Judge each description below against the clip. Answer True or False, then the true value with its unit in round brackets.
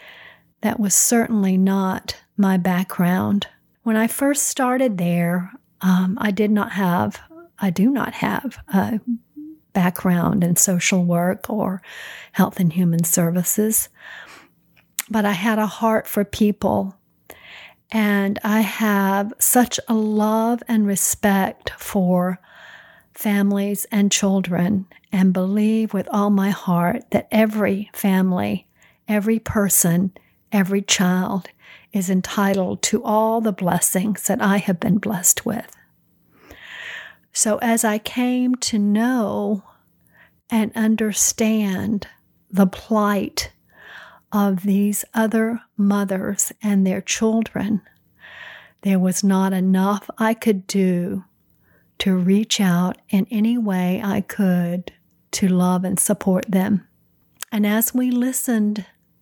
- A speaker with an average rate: False (115 wpm)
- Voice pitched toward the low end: False (200 Hz)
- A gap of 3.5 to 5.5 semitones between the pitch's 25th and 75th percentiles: False (2.7 semitones)